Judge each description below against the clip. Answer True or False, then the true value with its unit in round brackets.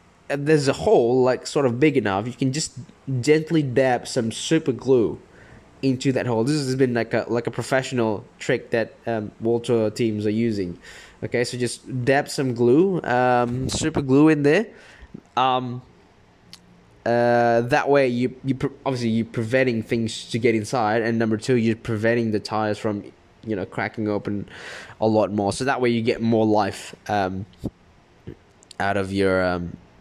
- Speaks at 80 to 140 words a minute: False (170 wpm)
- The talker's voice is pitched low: True (120 Hz)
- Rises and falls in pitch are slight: False (3.4 semitones)